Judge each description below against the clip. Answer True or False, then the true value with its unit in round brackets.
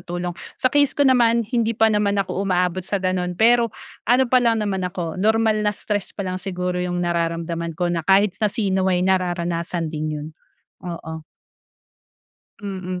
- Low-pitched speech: False (185 Hz)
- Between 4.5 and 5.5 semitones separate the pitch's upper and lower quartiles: False (3.4 semitones)